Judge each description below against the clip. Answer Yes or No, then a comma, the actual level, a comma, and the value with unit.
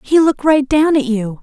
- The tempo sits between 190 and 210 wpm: No, fast, 255 wpm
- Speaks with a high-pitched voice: Yes, very high, 275 Hz